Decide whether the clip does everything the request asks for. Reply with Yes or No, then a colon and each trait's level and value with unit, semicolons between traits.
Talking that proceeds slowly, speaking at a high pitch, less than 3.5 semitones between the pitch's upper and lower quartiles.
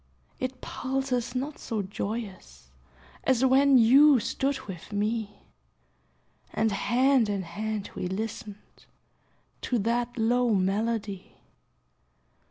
No: slow, 100 wpm; high, 225 Hz; average, 3.8 semitones